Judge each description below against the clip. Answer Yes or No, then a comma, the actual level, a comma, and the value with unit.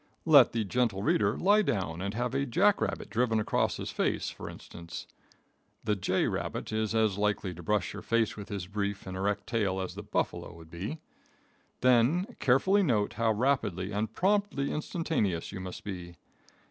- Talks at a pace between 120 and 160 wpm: No, average, 170 wpm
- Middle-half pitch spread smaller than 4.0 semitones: No, average, 4.6 semitones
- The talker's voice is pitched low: Yes, low, 105 Hz